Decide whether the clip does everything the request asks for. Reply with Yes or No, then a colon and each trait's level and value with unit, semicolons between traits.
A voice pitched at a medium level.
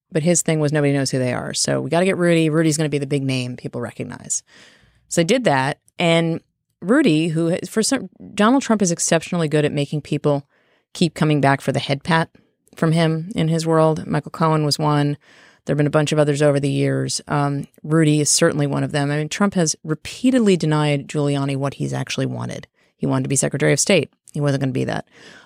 Yes: medium, 150 Hz